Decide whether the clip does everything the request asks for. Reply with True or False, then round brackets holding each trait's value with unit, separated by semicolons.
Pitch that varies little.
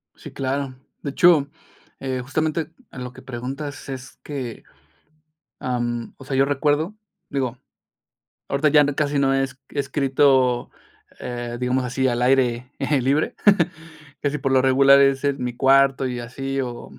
True (1.9 semitones)